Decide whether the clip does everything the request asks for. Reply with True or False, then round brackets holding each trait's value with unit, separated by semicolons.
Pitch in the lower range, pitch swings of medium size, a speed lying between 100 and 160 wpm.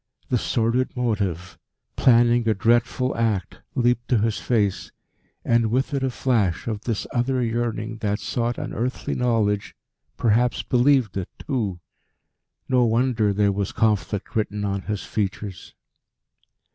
True (115 Hz; 3.0 semitones; 135 wpm)